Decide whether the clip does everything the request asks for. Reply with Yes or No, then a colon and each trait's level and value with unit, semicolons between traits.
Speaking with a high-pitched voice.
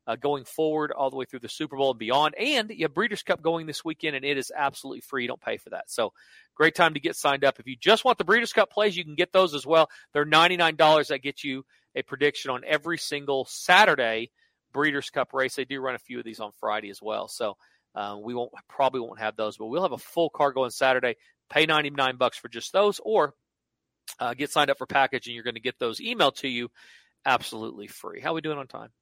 No: medium, 140 Hz